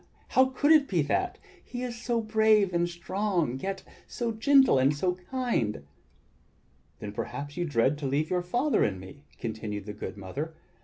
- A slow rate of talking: No, average, 170 wpm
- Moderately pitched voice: Yes, medium, 175 Hz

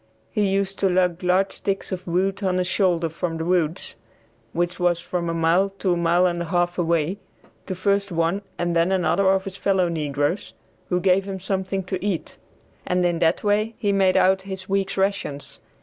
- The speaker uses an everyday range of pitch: No, narrow, 2.1 semitones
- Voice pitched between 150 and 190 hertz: Yes, medium, 185 Hz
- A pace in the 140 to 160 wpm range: No, average, 195 wpm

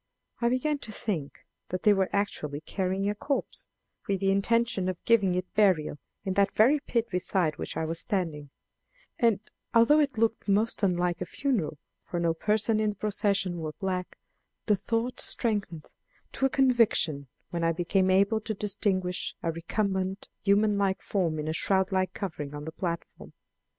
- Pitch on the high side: Yes, high, 195 Hz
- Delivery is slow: No, average, 170 wpm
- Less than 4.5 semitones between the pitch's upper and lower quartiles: Yes, average, 3.7 semitones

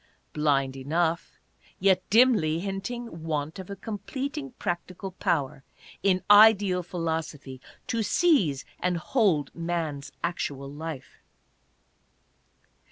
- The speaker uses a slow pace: Yes, slow, 100 wpm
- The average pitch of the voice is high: No, medium, 175 Hz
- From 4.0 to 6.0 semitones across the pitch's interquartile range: Yes, average, 5.0 semitones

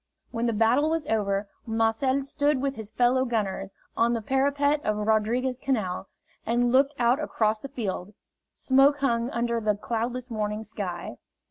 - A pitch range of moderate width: Yes, average, 3.8 semitones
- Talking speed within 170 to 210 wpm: No, average, 155 wpm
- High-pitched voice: Yes, high, 235 Hz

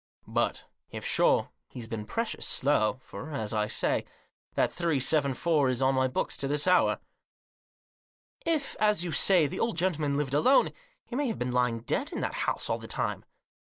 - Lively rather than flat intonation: Yes, wide, 6.0 semitones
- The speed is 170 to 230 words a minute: Yes, average, 195 wpm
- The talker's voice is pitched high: No, medium, 145 Hz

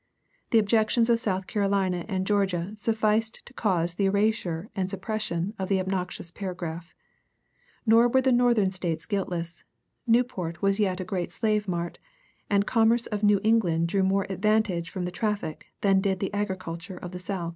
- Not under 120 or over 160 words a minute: No, average, 170 wpm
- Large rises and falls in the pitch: No, average, 3.1 semitones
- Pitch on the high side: Yes, high, 195 Hz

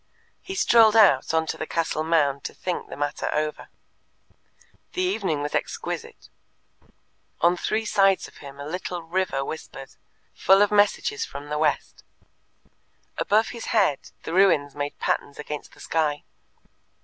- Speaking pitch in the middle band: Yes, medium, 165 Hz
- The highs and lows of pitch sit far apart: Yes, wide, 5.7 semitones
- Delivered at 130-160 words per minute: Yes, average, 150 wpm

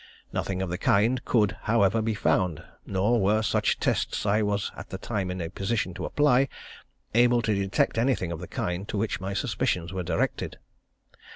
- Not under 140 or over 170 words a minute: No, average, 190 wpm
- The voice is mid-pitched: No, low, 100 Hz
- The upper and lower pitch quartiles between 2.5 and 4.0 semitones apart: Yes, average, 3.4 semitones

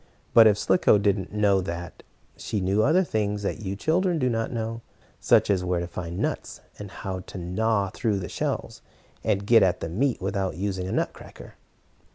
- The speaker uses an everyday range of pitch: Yes, average, 3.2 semitones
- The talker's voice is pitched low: Yes, low, 100 Hz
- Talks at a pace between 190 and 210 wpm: Yes, average, 200 wpm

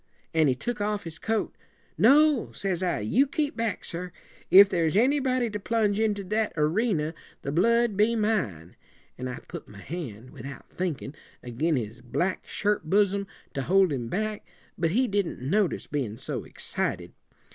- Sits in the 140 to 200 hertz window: Yes, high, 190 Hz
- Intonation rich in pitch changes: Yes, wide, 6.3 semitones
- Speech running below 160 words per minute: No, average, 165 wpm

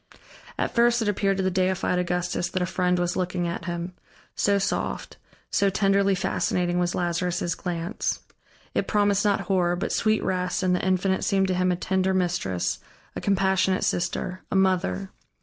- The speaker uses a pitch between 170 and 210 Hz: Yes, medium, 185 Hz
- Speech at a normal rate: Yes, average, 170 wpm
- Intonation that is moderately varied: No, narrow, 1.6 semitones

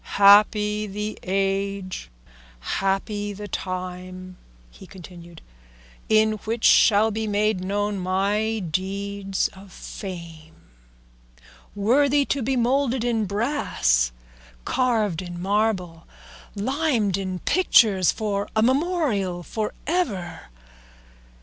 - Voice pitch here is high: Yes, high, 200 Hz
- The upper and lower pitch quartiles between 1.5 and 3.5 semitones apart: Yes, average, 3.1 semitones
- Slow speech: Yes, slow, 100 wpm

